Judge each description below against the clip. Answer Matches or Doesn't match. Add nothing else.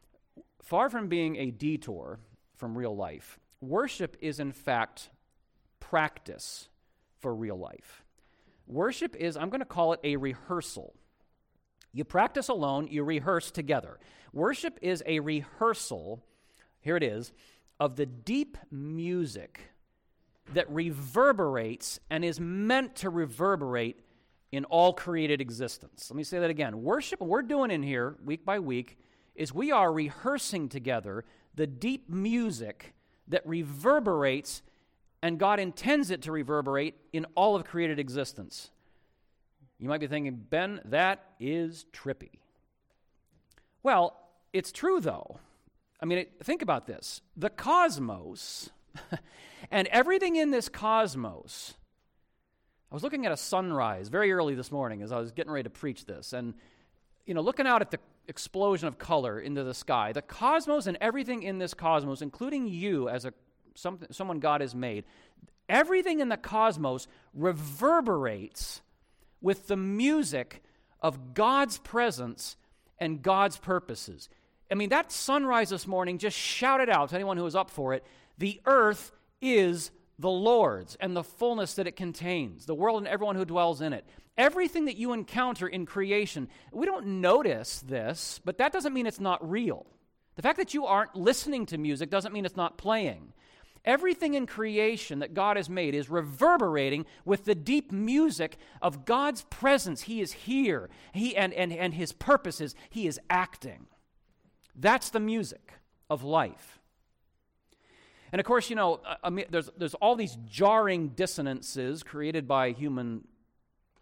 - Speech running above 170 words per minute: Doesn't match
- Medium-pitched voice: Matches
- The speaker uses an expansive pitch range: Matches